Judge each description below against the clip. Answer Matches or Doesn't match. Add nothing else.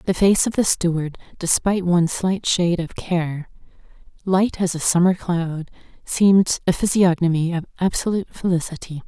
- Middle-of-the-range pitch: Matches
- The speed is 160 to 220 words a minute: Doesn't match